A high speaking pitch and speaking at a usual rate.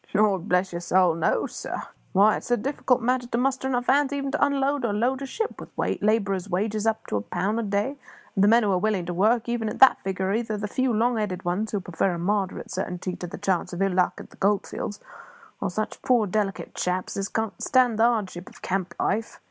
No: high, 210 Hz; fast, 240 wpm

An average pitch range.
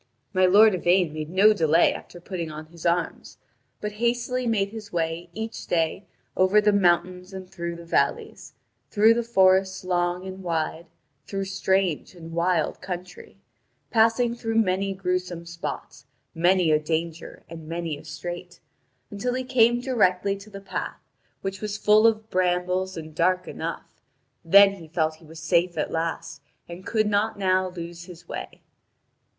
Yes: average, 3.1 semitones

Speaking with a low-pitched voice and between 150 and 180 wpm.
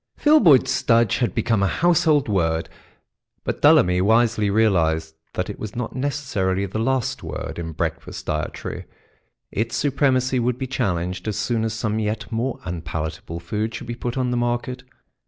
Yes: low, 110 Hz; average, 160 wpm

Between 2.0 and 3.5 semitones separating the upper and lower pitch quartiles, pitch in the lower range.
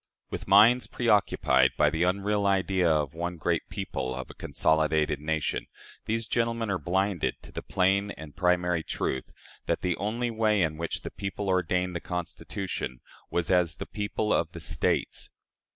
No: average, 4.3 semitones; very low, 90 Hz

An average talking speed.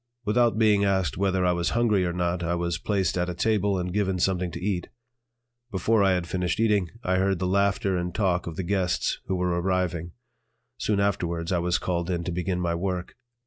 No: fast, 210 wpm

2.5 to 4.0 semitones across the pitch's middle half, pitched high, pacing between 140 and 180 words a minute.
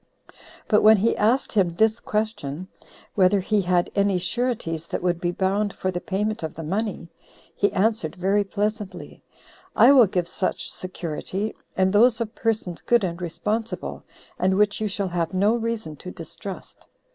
Yes: average, 3.3 semitones; high, 200 Hz; average, 165 wpm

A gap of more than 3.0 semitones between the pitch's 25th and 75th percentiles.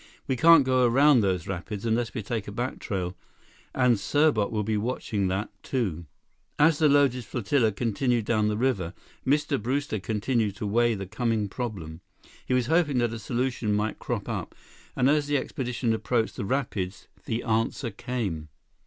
Yes: average, 4.0 semitones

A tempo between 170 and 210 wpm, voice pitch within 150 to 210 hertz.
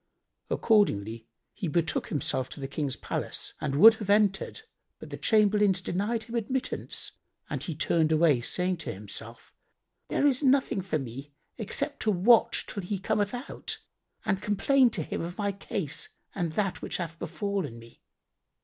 No: average, 160 wpm; high, 190 Hz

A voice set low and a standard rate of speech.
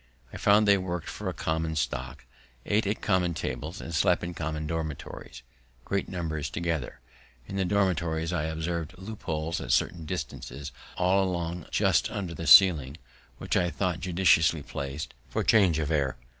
Yes: very low, 85 Hz; average, 160 wpm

